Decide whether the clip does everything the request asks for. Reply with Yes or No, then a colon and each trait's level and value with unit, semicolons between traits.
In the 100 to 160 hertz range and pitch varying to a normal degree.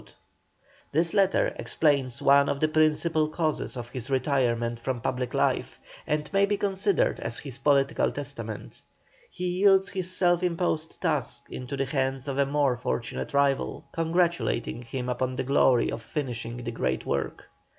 Yes: medium, 140 Hz; average, 4.6 semitones